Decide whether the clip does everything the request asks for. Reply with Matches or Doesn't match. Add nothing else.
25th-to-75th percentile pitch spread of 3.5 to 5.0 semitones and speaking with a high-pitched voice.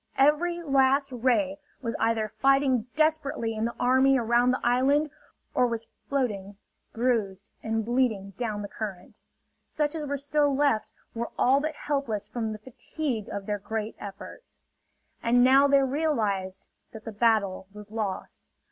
Matches